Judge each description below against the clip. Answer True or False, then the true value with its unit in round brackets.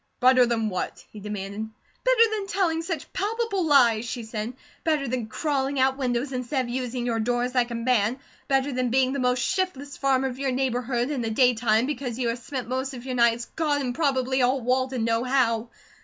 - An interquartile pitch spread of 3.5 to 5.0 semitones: False (2.5 semitones)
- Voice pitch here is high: True (255 Hz)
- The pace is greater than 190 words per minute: True (200 wpm)